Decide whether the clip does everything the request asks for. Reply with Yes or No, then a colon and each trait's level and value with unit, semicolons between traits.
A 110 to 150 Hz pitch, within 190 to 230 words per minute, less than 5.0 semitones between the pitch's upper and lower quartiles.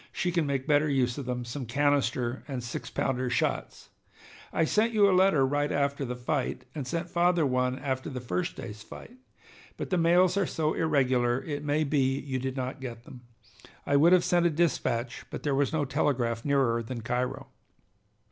Yes: medium, 140 Hz; average, 195 wpm; average, 3.7 semitones